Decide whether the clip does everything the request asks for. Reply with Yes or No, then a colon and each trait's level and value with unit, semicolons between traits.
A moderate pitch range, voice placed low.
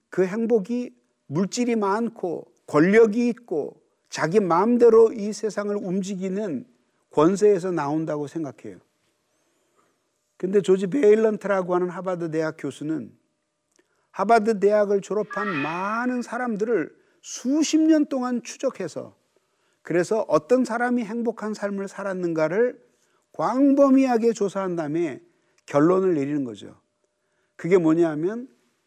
No: average, 4.7 semitones; high, 205 Hz